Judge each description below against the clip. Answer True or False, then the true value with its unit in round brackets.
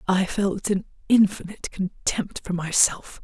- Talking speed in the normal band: False (130 wpm)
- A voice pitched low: False (190 Hz)